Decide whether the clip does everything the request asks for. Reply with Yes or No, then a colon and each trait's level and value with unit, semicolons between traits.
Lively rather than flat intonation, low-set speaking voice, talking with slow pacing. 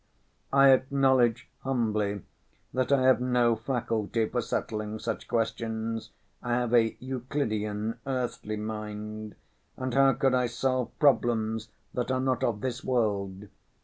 No: average, 3.0 semitones; low, 120 Hz; slow, 130 wpm